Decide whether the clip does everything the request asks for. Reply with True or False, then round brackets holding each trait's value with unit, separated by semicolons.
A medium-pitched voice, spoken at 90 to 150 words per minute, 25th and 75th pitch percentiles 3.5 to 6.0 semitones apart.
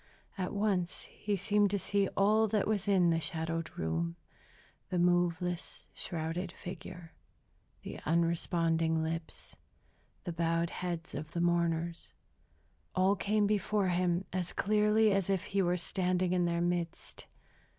False (175 Hz; 135 wpm; 2.8 semitones)